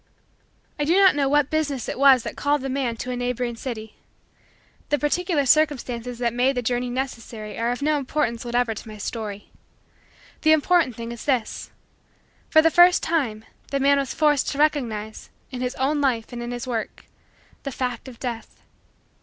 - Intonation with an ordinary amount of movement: Yes, average, 3.6 semitones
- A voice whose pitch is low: No, very high, 255 Hz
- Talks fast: No, average, 185 wpm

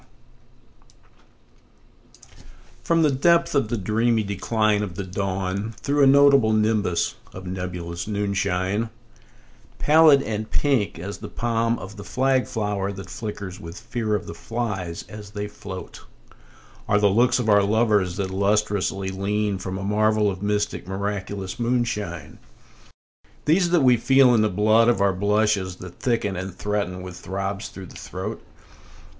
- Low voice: Yes, low, 105 Hz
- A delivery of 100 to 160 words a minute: Yes, average, 150 wpm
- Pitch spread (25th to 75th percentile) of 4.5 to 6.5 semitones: No, average, 3.2 semitones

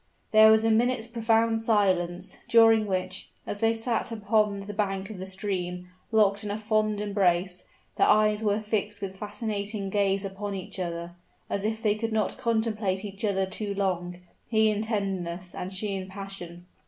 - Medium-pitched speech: No, high, 205 Hz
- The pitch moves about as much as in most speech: No, narrow, 2.3 semitones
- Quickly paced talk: No, average, 175 wpm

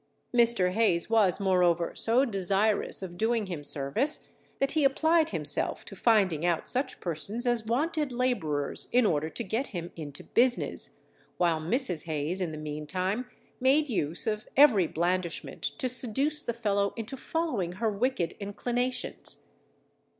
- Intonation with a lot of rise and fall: Yes, wide, 6.2 semitones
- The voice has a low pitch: No, high, 210 Hz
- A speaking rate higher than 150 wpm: No, average, 145 wpm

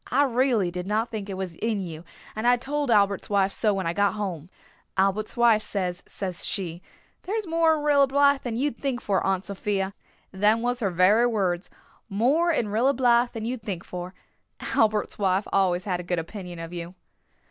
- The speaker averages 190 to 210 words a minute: Yes, average, 195 wpm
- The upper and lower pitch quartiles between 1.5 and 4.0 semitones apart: No, average, 4.5 semitones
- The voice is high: Yes, high, 210 Hz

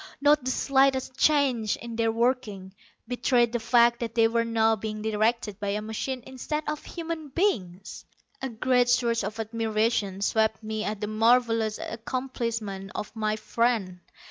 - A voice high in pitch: Yes, high, 230 Hz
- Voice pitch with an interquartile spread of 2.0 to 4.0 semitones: Yes, average, 2.7 semitones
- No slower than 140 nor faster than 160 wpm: Yes, average, 155 wpm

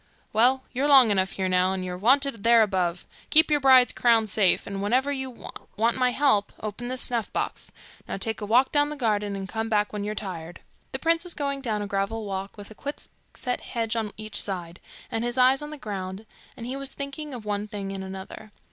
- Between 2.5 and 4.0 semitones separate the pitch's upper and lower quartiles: No, average, 4.6 semitones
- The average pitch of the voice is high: Yes, high, 220 Hz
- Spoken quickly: Yes, fast, 220 wpm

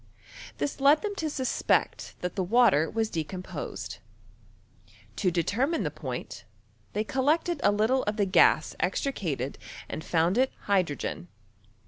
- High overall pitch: Yes, high, 205 Hz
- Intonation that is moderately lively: No, wide, 7.3 semitones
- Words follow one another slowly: Yes, slow, 130 wpm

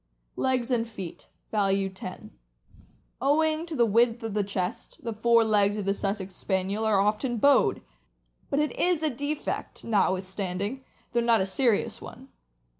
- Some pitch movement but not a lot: Yes, average, 4.0 semitones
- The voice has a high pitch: Yes, high, 220 Hz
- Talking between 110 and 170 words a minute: Yes, average, 155 wpm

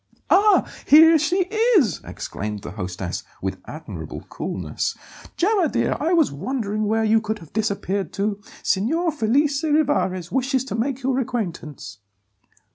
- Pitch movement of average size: No, wide, 7.7 semitones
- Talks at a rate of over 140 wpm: No, slow, 135 wpm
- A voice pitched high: Yes, high, 225 Hz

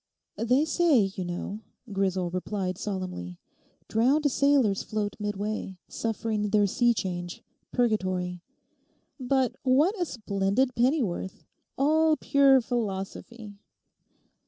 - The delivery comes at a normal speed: No, slow, 100 wpm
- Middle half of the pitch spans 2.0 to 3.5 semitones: No, average, 5.3 semitones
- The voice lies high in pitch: Yes, high, 215 Hz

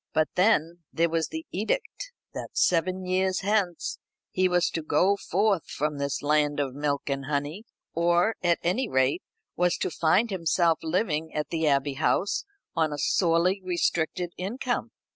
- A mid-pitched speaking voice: Yes, medium, 170 Hz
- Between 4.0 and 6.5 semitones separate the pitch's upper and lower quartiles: No, average, 3.6 semitones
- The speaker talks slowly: No, average, 160 wpm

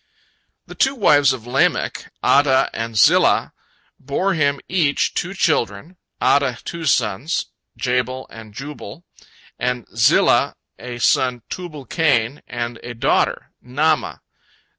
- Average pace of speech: No, slow, 120 wpm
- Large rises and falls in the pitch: No, average, 4.2 semitones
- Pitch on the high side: No, low, 130 Hz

